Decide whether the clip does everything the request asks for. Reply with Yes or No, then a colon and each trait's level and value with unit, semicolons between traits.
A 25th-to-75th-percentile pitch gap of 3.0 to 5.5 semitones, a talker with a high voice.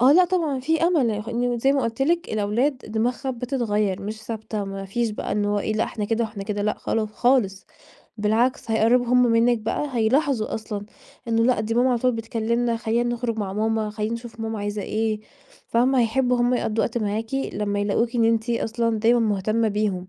No: narrow, 2.4 semitones; high, 225 Hz